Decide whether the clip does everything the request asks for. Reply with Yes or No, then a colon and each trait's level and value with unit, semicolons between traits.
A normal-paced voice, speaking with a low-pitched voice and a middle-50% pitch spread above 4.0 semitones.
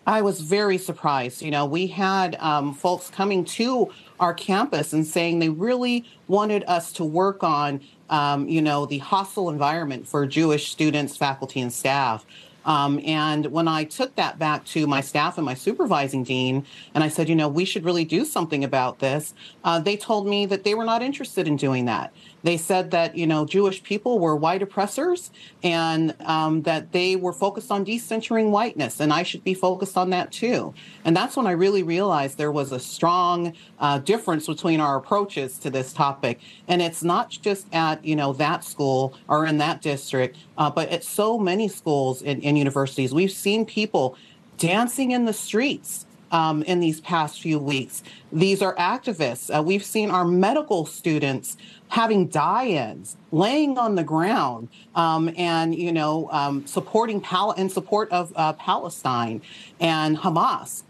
No: average, 180 wpm; medium, 170 Hz; average, 4.8 semitones